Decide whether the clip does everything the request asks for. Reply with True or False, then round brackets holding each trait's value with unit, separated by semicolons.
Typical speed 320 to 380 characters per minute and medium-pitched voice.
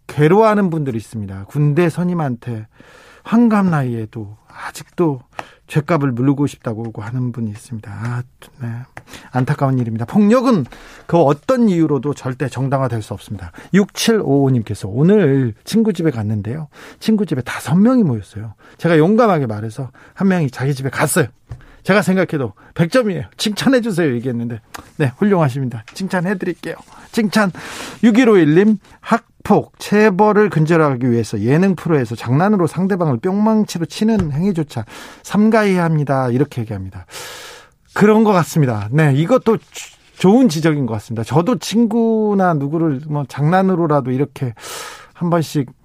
True (325 characters per minute; 150 Hz)